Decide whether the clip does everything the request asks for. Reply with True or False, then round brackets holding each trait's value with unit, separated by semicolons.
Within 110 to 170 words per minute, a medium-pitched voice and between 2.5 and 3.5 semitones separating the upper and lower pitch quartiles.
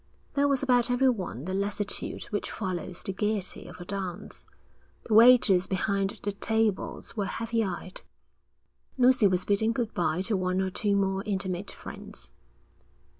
False (150 wpm; 200 Hz; 3.2 semitones)